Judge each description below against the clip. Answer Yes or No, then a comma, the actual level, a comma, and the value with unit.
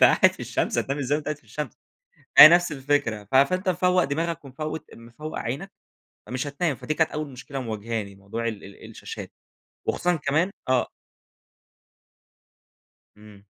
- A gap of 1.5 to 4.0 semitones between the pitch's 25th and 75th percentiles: No, average, 5.1 semitones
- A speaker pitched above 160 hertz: No, medium, 140 Hz